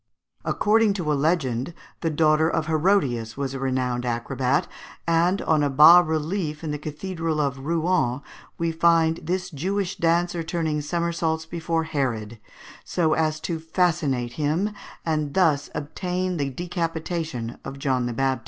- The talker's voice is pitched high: No, medium, 160 Hz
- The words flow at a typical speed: Yes, average, 145 wpm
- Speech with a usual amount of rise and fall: Yes, average, 3.6 semitones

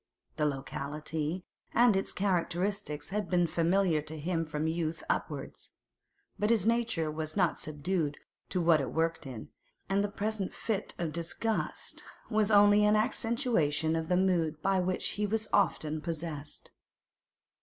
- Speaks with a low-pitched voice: No, medium, 175 Hz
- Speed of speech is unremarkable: Yes, average, 145 wpm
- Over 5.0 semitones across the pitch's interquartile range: No, average, 4.6 semitones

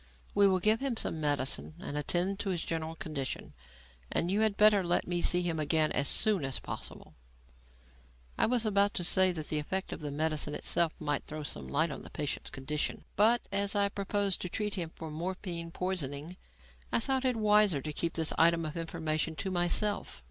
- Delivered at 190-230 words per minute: Yes, average, 200 wpm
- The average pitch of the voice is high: No, medium, 175 Hz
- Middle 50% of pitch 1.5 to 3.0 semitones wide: No, average, 4.5 semitones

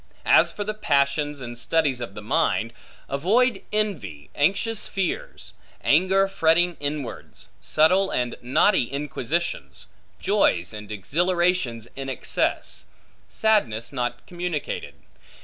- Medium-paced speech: No, slow, 110 wpm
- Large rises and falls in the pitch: Yes, wide, 7.1 semitones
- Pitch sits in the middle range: Yes, medium, 150 Hz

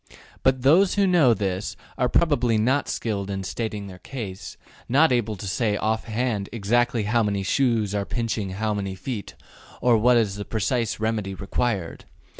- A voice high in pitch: No, low, 110 Hz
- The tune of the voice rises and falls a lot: No, average, 3.5 semitones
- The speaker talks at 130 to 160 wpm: No, average, 175 wpm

